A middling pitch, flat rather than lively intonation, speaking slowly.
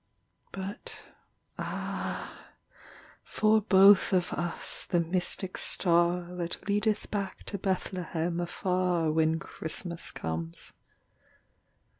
Yes: medium, 180 Hz; narrow, 2.3 semitones; slow, 90 wpm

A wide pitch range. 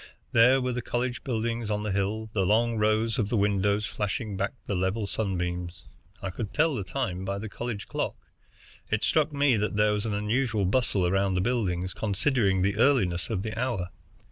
No: average, 3.3 semitones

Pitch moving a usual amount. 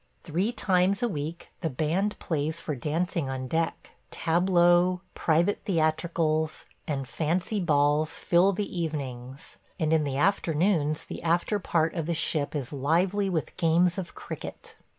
Yes: average, 3.0 semitones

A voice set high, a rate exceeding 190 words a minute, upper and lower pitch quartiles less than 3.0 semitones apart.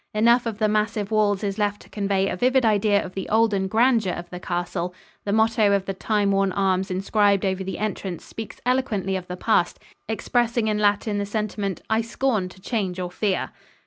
Yes: high, 205 Hz; average, 200 wpm; narrow, 2.5 semitones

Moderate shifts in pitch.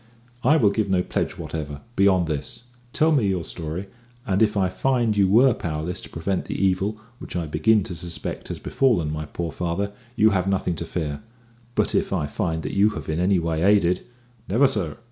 Yes: average, 4.2 semitones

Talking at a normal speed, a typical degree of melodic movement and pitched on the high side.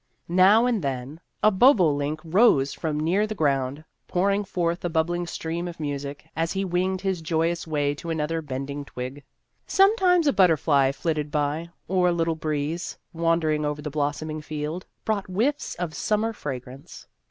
No: average, 170 wpm; average, 4.0 semitones; medium, 165 Hz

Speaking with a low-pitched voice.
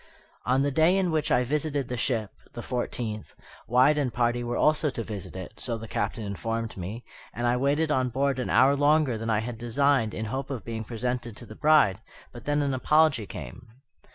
Yes: low, 125 Hz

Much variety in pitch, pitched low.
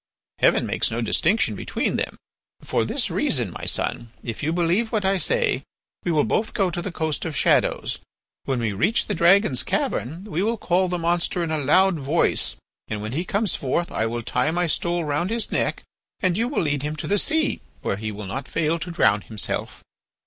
No: wide, 6.2 semitones; medium, 170 Hz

